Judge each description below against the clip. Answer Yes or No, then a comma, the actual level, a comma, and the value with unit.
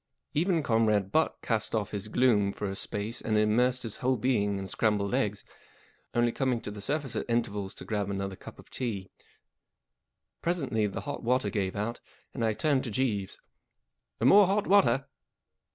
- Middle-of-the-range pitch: No, low, 110 Hz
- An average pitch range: Yes, average, 4.2 semitones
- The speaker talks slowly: No, average, 175 wpm